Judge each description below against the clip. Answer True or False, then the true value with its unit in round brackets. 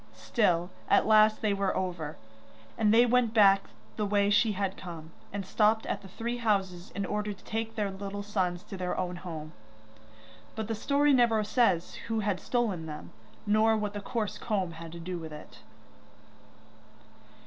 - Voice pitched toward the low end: False (205 Hz)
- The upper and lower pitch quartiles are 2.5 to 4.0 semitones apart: True (3.3 semitones)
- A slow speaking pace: False (175 wpm)